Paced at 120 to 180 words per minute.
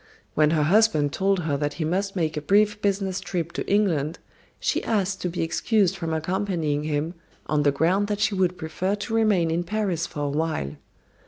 No: average, 195 wpm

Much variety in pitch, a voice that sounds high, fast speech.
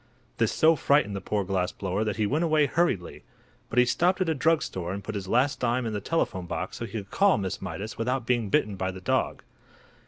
No: wide, 6.6 semitones; low, 110 Hz; fast, 245 wpm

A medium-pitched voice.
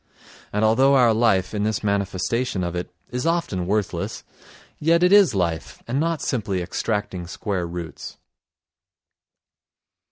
No: low, 105 Hz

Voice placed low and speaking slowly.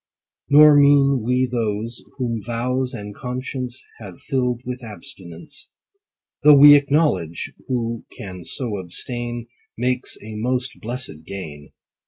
Yes: low, 120 Hz; slow, 120 wpm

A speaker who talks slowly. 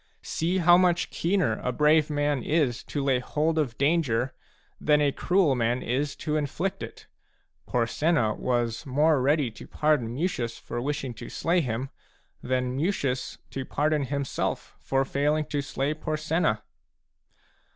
No: average, 150 wpm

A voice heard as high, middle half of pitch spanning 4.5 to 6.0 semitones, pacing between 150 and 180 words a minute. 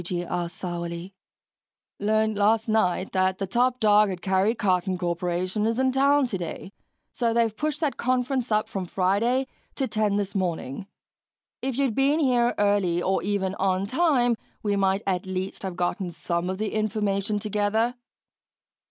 No: high, 205 Hz; average, 3.9 semitones; average, 160 wpm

